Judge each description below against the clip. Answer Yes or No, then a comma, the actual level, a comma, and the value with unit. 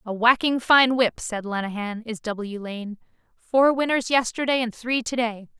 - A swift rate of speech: No, average, 160 wpm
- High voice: Yes, high, 235 Hz